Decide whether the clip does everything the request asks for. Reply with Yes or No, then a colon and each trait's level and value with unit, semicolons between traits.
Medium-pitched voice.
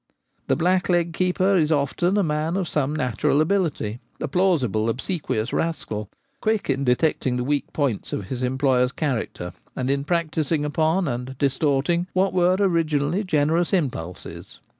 Yes: medium, 150 Hz